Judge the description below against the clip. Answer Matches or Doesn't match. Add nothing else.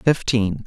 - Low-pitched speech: Matches